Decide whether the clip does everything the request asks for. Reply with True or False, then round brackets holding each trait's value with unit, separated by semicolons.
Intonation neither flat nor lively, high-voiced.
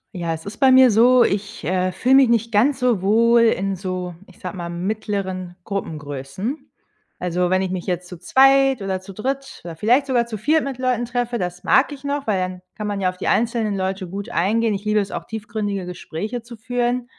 True (4.7 semitones; 210 Hz)